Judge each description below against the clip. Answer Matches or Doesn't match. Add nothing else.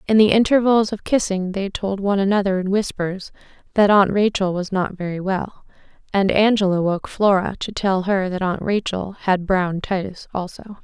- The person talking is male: Doesn't match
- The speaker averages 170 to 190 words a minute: Matches